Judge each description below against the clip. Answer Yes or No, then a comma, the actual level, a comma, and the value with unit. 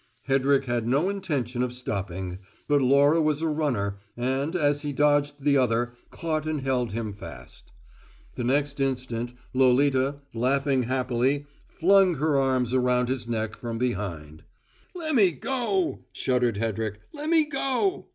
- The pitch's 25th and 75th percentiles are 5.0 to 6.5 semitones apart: No, average, 3.6 semitones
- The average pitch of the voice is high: No, low, 135 Hz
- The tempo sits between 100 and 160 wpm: Yes, average, 140 wpm